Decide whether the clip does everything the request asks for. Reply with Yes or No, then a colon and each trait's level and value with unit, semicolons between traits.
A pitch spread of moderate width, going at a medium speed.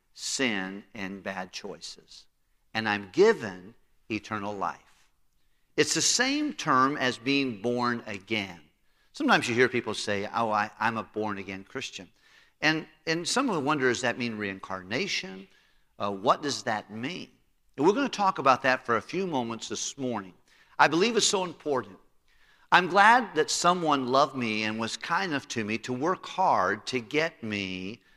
No: wide, 6.3 semitones; average, 170 wpm